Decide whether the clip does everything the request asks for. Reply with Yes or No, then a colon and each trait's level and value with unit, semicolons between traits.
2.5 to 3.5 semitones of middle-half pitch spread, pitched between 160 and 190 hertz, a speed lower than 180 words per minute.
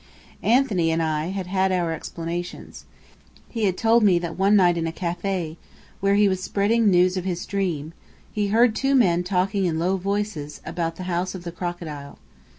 No: average, 2.8 semitones; medium, 185 Hz; average, 195 wpm